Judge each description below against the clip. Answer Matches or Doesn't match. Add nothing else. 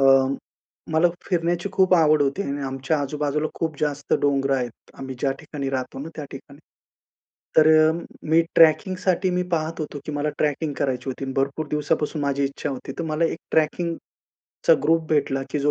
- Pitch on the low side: Doesn't match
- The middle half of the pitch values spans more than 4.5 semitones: Doesn't match